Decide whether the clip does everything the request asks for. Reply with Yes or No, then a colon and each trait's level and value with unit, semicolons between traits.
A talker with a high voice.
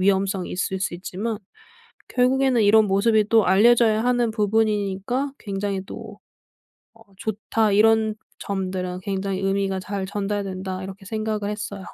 Yes: high, 205 Hz